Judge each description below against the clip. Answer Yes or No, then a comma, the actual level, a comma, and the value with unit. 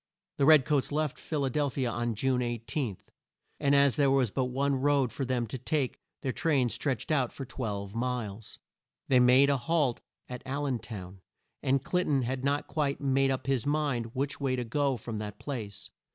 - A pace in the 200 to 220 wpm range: Yes, fast, 205 wpm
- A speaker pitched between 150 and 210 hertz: No, low, 130 Hz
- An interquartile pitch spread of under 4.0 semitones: Yes, average, 2.9 semitones